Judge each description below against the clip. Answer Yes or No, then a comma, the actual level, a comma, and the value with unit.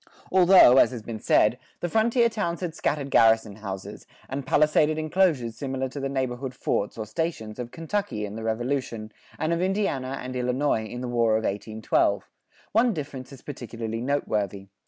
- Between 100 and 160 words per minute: No, average, 170 wpm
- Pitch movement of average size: No, wide, 5.8 semitones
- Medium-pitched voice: No, low, 130 Hz